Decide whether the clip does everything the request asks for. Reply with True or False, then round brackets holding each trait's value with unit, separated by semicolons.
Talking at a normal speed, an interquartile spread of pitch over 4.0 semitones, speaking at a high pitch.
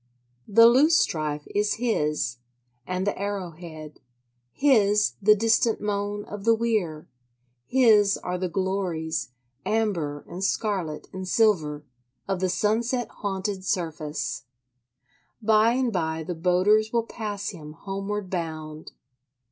False (120 wpm; 4.8 semitones; 195 Hz)